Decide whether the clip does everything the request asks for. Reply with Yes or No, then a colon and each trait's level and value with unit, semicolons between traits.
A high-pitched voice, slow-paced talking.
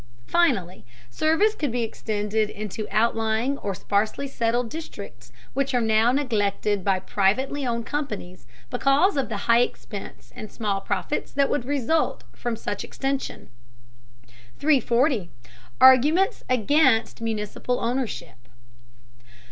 Yes: high, 230 Hz; slow, 115 wpm